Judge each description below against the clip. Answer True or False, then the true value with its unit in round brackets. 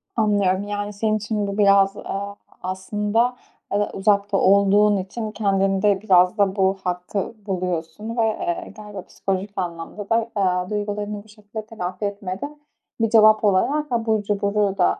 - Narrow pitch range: True (1.8 semitones)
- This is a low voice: False (205 Hz)